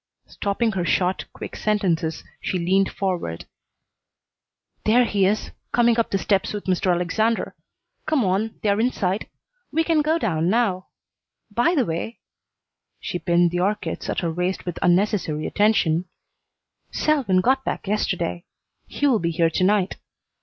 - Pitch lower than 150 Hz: No, high, 195 Hz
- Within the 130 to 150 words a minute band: Yes, average, 145 wpm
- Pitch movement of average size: Yes, average, 4.1 semitones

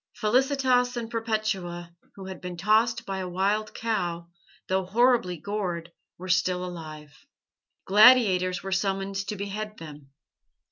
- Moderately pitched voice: No, high, 195 Hz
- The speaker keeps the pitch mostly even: No, average, 3.5 semitones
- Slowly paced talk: Yes, slow, 130 wpm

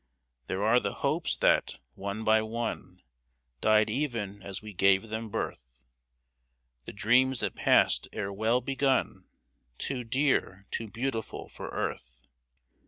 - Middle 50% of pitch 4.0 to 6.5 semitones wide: No, average, 3.6 semitones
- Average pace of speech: No, slow, 130 wpm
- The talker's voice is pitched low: Yes, low, 110 Hz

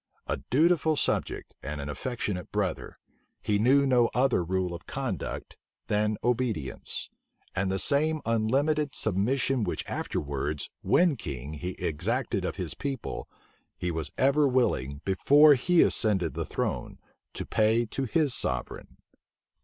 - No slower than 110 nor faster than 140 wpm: Yes, slow, 135 wpm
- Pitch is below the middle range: Yes, low, 110 Hz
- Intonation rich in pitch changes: Yes, wide, 7.4 semitones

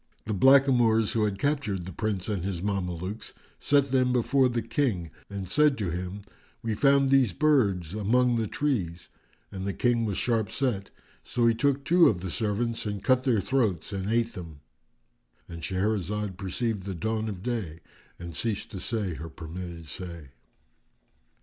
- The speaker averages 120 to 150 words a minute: No, average, 165 wpm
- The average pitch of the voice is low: Yes, low, 105 Hz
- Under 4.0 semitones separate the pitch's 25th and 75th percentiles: No, average, 4.8 semitones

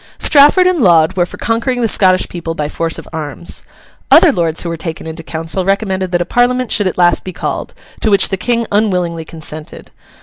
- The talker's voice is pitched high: No, medium, 180 Hz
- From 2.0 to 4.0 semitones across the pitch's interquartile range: No, average, 4.9 semitones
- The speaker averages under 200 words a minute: No, fast, 205 wpm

